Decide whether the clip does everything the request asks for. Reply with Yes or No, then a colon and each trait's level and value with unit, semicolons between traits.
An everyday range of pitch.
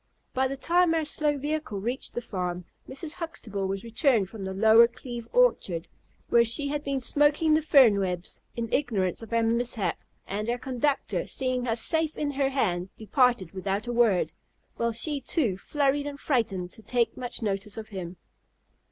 No: wide, 5.8 semitones